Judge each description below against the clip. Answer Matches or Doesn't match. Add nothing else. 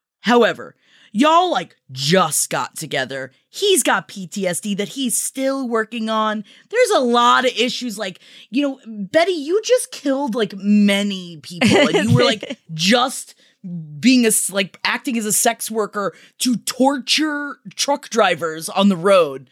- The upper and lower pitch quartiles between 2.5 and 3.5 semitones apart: Doesn't match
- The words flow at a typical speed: Matches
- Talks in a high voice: Matches